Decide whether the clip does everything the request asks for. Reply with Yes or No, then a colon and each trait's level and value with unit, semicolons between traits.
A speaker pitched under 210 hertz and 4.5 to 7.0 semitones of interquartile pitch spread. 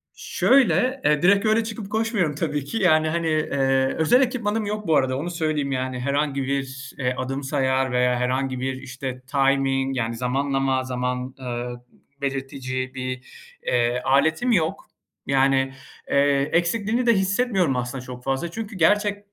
Yes: medium, 140 Hz; average, 5.3 semitones